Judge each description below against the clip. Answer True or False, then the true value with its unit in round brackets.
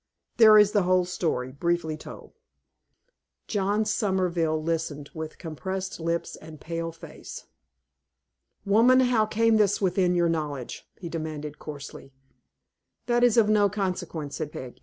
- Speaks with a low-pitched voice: False (175 Hz)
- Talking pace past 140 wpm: False (135 wpm)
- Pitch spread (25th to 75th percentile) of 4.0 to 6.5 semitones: True (4.6 semitones)